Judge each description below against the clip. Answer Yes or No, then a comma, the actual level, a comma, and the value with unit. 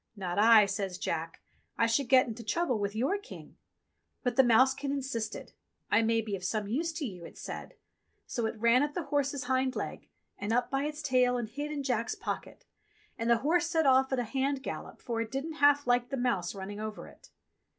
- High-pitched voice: Yes, high, 245 Hz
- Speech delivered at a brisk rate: Yes, fast, 215 wpm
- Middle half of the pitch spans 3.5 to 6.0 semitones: Yes, average, 4.0 semitones